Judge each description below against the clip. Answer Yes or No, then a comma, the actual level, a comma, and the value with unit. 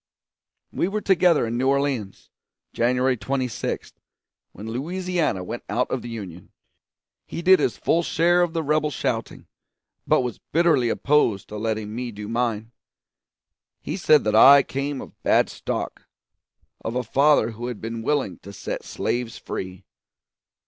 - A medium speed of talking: Yes, average, 150 wpm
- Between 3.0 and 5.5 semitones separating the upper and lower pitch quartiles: Yes, average, 5.2 semitones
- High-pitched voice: No, low, 125 Hz